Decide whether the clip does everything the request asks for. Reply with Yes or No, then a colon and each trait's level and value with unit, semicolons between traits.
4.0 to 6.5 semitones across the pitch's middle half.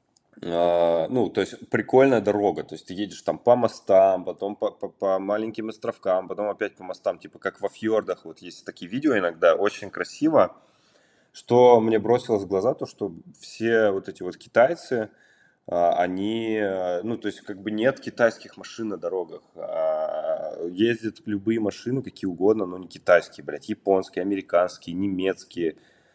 No: average, 3.2 semitones